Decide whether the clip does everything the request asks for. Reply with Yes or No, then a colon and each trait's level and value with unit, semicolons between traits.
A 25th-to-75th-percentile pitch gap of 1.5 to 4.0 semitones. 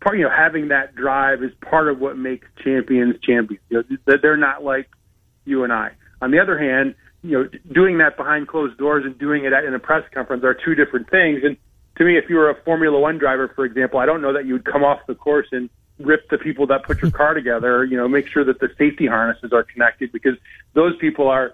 Yes: average, 2.8 semitones